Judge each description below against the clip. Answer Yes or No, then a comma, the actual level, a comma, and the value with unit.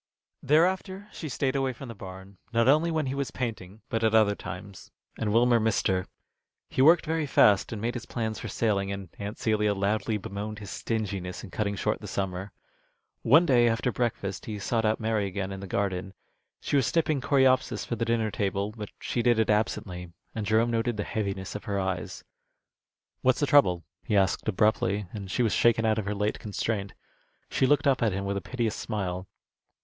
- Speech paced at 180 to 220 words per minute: Yes, average, 200 wpm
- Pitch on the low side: Yes, low, 110 Hz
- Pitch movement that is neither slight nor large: Yes, average, 3.4 semitones